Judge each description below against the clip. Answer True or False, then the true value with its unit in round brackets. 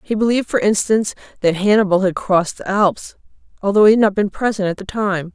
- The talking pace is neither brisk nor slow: False (215 wpm)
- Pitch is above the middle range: True (200 Hz)